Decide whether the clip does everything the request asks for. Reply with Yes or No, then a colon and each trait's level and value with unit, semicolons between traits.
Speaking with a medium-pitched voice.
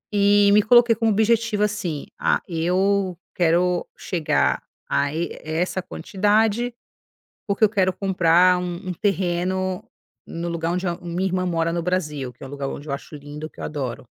Yes: medium, 180 Hz